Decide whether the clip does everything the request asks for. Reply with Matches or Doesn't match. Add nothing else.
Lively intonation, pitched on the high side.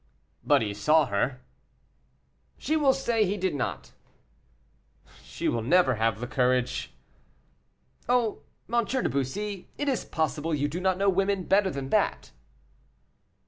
Doesn't match